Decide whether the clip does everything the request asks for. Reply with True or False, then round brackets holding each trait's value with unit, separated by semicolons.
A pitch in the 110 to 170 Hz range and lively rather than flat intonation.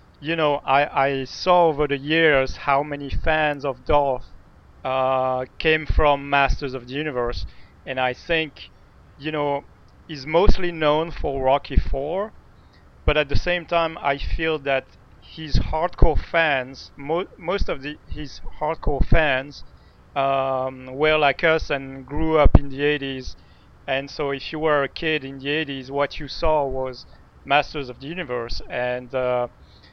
False (140 Hz; 2.7 semitones)